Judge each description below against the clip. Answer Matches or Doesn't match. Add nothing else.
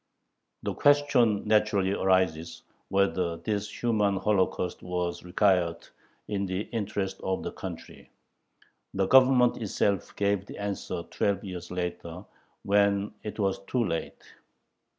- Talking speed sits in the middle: Doesn't match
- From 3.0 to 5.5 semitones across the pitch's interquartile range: Doesn't match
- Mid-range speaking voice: Doesn't match